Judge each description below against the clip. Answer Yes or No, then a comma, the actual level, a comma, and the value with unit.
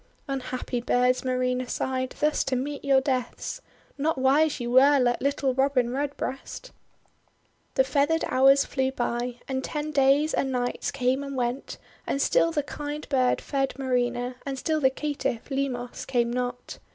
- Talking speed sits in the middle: Yes, average, 160 wpm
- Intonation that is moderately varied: No, narrow, 2.0 semitones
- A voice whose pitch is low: No, very high, 265 Hz